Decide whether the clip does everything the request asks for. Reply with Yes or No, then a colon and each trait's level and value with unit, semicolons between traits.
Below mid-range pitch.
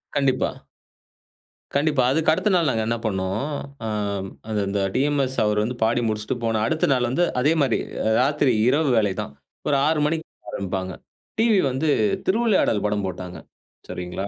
Yes: low, 125 Hz